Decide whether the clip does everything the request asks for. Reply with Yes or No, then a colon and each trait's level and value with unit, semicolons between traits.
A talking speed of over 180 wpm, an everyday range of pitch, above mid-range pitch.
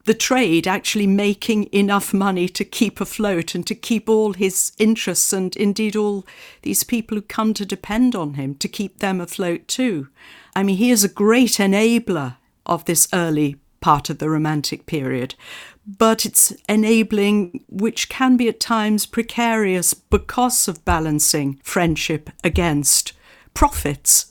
No: average, 150 wpm; average, 4.3 semitones; high, 200 Hz